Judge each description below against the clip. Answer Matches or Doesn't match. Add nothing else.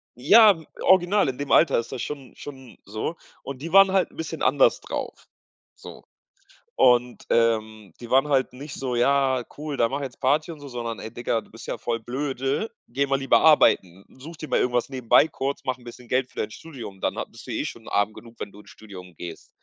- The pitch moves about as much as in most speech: Matches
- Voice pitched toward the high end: Doesn't match